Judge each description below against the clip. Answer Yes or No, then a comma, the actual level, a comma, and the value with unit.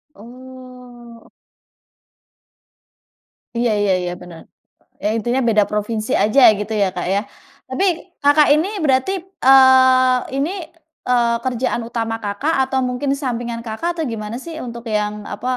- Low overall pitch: No, high, 240 Hz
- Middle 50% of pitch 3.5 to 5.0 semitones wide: No, average, 3.0 semitones